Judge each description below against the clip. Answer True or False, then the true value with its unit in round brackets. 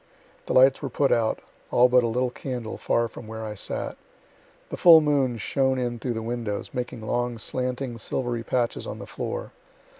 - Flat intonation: True (2.0 semitones)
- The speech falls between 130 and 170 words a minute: False (185 wpm)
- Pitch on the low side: True (120 Hz)